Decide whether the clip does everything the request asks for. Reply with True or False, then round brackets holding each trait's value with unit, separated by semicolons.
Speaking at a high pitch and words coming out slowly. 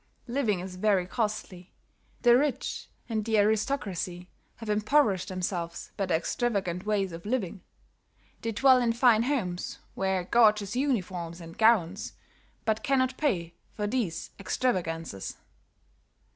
True (210 Hz; 125 wpm)